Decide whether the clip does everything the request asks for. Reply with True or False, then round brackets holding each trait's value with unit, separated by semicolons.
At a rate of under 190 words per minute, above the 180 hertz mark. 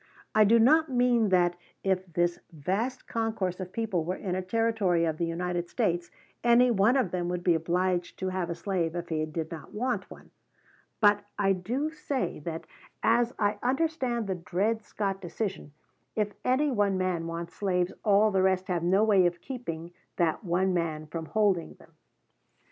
True (180 wpm; 190 Hz)